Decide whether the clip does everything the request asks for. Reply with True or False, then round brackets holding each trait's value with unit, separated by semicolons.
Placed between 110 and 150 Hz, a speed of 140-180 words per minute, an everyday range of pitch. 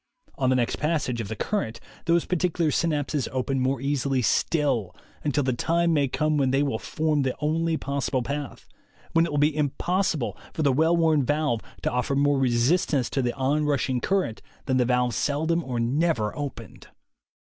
False (140 Hz; 190 wpm; 3.5 semitones)